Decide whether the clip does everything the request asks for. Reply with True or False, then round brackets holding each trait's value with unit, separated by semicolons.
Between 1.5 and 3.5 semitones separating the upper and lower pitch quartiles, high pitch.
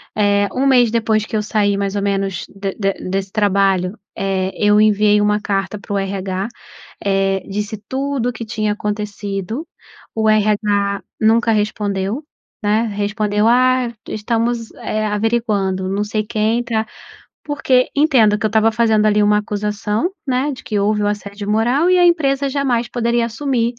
True (2.5 semitones; 215 Hz)